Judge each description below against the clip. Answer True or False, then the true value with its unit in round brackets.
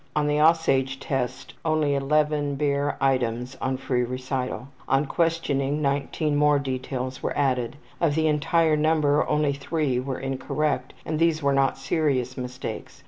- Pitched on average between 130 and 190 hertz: True (140 Hz)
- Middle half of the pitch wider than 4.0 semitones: False (2.5 semitones)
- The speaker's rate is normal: True (155 wpm)